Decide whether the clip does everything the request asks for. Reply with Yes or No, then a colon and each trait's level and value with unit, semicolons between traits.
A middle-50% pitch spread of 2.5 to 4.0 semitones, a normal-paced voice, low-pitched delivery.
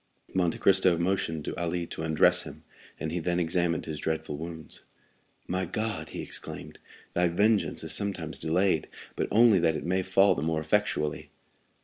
Yes: average, 2.8 semitones; average, 165 wpm; very low, 85 Hz